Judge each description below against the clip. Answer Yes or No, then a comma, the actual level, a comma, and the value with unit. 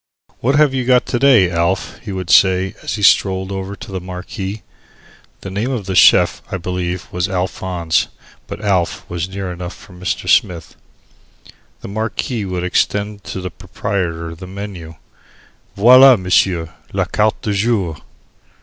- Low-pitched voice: Yes, very low, 95 Hz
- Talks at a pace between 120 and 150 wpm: No, average, 160 wpm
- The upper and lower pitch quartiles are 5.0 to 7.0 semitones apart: No, narrow, 2.5 semitones